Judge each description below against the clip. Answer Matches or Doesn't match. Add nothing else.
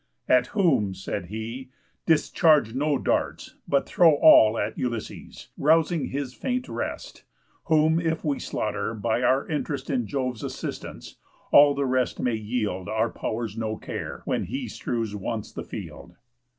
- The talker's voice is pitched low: Matches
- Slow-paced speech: Doesn't match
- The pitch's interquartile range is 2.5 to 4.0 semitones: Doesn't match